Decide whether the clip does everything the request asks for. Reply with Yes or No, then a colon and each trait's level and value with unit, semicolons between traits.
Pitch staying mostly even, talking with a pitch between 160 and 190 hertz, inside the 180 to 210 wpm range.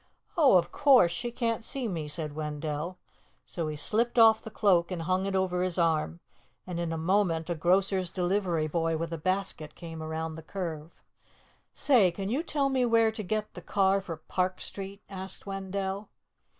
No: average, 3.7 semitones; medium, 185 Hz; average, 185 wpm